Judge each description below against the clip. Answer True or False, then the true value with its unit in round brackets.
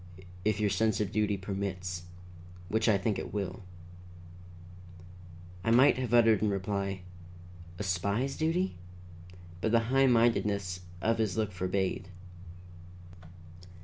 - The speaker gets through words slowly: True (120 wpm)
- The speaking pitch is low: True (105 Hz)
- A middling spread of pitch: True (3.0 semitones)